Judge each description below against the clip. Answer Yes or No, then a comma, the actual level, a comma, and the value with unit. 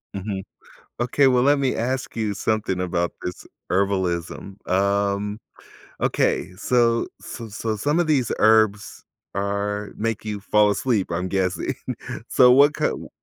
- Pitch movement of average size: Yes, average, 3.4 semitones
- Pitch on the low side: Yes, low, 105 Hz